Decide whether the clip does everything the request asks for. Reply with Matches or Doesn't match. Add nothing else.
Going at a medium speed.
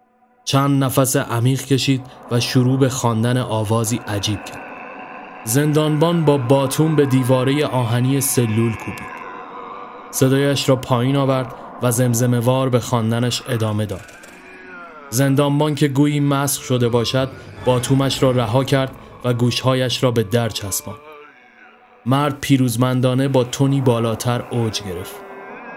Matches